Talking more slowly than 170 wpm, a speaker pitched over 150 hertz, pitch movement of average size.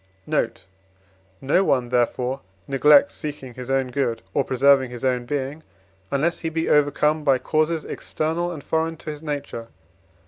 No: average, 150 wpm; medium, 140 Hz; average, 3.1 semitones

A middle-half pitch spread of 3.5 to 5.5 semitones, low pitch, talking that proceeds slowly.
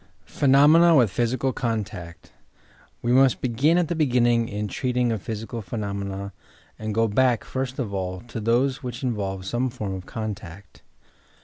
No: average, 4.2 semitones; low, 115 Hz; average, 155 wpm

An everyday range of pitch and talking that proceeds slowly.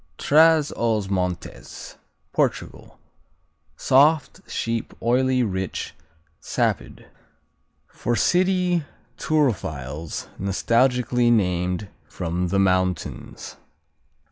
No: wide, 6.5 semitones; slow, 70 wpm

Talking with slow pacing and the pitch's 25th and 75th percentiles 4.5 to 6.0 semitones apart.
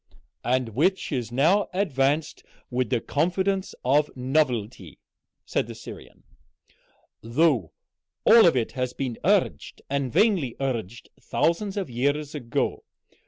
Yes: slow, 120 wpm; wide, 5.6 semitones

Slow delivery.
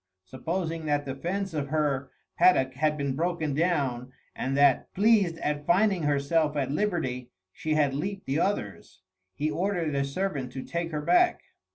No: average, 165 wpm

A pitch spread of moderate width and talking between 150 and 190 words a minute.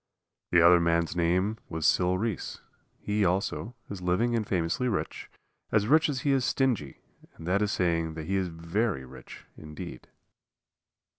Yes: average, 4.6 semitones; average, 160 wpm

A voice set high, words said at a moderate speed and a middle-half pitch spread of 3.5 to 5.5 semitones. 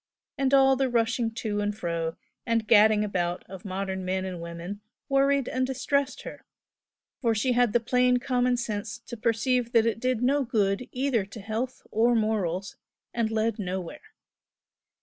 Yes: high, 225 Hz; average, 165 wpm; average, 3.9 semitones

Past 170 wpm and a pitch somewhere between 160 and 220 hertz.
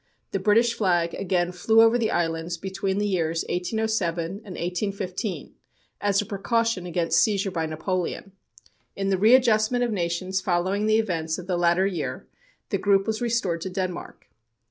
No: average, 160 wpm; high, 190 Hz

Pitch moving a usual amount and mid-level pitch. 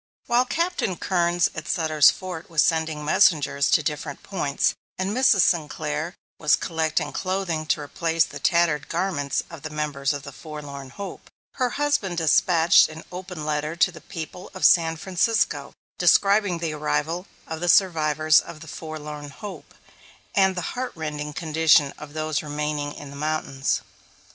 Yes: average, 3.0 semitones; medium, 160 Hz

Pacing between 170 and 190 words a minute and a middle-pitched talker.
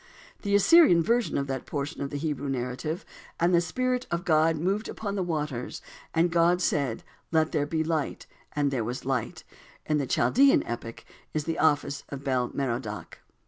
Yes: average, 180 wpm; medium, 155 Hz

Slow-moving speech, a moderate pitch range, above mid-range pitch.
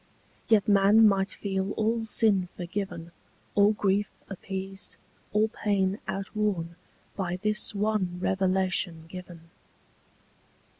No: slow, 100 wpm; narrow, 2.2 semitones; high, 195 Hz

